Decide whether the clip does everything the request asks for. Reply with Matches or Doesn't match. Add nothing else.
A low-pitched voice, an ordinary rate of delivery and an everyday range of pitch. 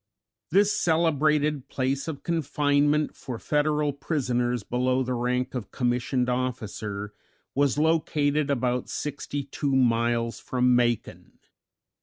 Doesn't match